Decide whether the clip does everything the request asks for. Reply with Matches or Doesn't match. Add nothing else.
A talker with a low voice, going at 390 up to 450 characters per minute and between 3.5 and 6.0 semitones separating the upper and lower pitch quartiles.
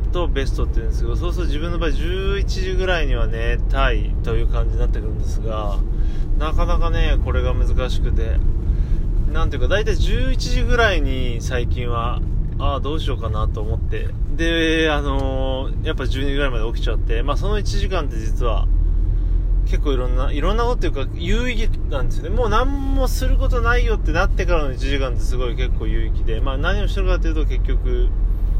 Matches